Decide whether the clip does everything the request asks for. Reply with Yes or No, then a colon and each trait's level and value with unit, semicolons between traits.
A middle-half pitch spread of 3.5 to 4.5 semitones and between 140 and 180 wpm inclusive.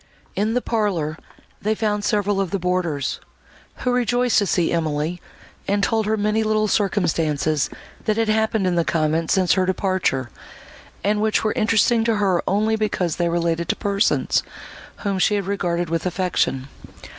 Yes: average, 3.9 semitones; average, 165 wpm